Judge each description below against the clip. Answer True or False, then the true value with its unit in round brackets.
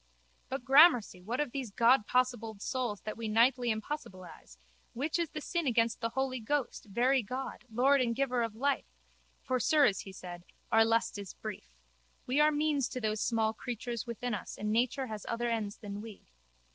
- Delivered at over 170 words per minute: True (180 wpm)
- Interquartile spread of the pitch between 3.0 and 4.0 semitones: True (3.5 semitones)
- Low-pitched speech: False (235 Hz)